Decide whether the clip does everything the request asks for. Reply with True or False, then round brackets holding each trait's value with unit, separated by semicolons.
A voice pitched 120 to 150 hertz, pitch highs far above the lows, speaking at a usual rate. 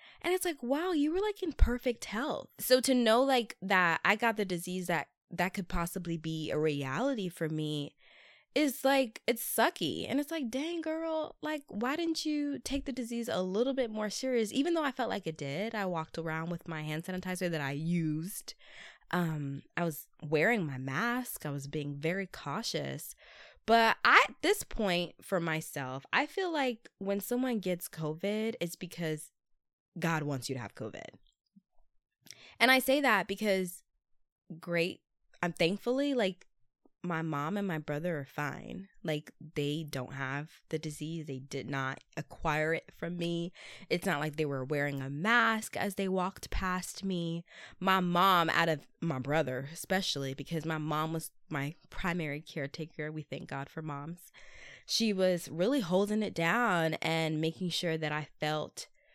False (175 Hz; 6.6 semitones; 175 wpm)